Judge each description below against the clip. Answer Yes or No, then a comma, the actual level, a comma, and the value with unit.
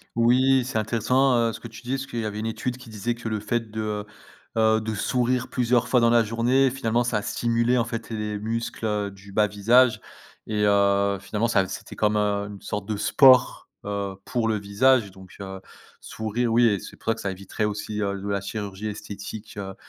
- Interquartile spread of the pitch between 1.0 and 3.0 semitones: Yes, average, 2.7 semitones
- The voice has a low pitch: Yes, low, 110 Hz